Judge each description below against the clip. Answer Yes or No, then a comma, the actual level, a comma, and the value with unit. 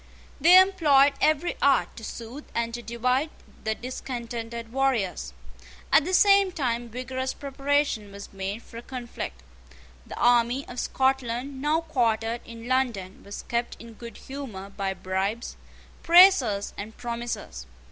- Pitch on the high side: Yes, high, 240 Hz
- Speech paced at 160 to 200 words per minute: No, slow, 135 wpm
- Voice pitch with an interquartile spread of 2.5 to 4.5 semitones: Yes, average, 3.3 semitones